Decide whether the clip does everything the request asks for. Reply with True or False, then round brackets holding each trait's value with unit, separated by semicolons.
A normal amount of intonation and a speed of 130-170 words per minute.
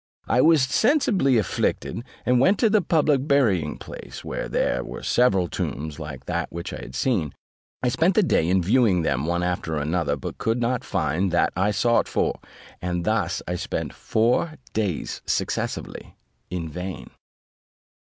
False (7.3 semitones; 165 wpm)